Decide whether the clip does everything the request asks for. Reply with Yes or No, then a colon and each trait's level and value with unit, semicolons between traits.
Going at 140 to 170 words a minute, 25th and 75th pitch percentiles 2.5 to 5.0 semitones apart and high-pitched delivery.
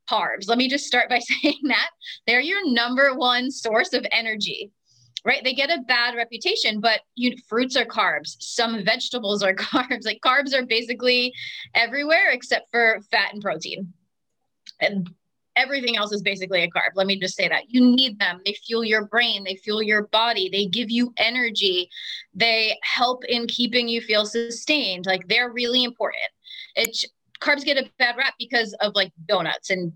No: average, 180 wpm; average, 3.4 semitones; high, 235 Hz